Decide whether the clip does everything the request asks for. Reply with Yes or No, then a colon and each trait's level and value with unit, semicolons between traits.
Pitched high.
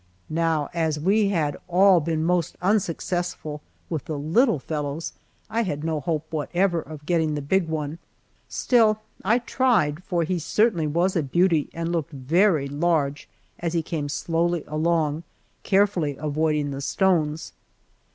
No: medium, 165 Hz